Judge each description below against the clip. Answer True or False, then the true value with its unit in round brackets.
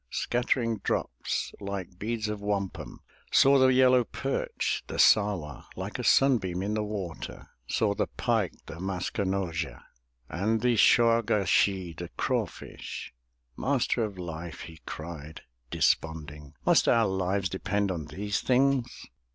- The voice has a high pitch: False (100 Hz)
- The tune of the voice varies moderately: True (4.6 semitones)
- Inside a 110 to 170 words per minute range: True (145 wpm)